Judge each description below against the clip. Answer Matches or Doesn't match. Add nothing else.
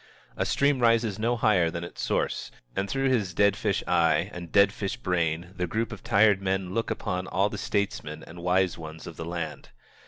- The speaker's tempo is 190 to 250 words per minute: Matches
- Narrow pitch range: Doesn't match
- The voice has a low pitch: Matches